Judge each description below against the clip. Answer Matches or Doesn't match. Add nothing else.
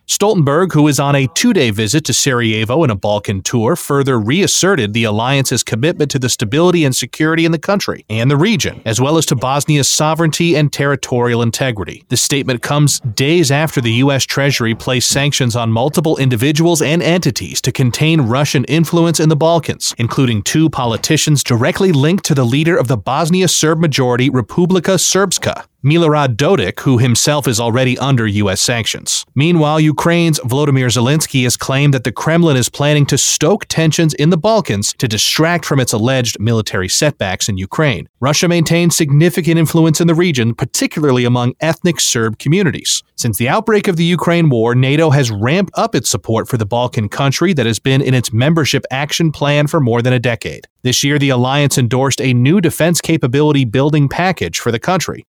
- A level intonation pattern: Doesn't match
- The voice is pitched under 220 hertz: Matches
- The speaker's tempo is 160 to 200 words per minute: Matches